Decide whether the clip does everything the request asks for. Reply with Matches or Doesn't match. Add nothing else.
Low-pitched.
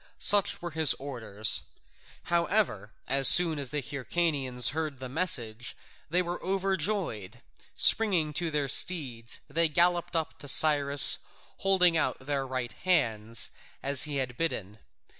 Doesn't match